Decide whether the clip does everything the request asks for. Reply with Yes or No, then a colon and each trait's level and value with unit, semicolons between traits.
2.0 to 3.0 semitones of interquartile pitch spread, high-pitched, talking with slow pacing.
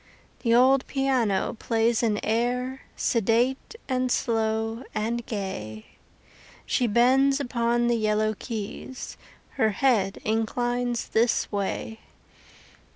Yes: narrow, 2.4 semitones; high, 235 Hz; slow, 100 wpm